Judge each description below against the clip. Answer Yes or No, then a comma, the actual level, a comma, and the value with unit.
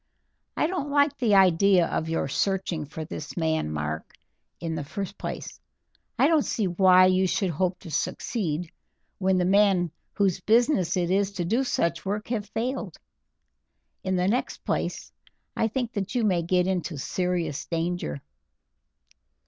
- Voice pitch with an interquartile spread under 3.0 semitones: No, average, 3.7 semitones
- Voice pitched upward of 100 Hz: Yes, medium, 185 Hz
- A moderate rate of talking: Yes, average, 155 wpm